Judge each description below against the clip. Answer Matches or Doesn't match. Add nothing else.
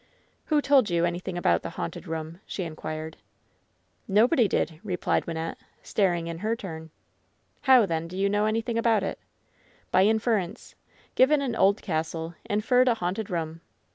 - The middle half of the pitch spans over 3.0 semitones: Matches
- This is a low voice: Doesn't match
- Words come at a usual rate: Matches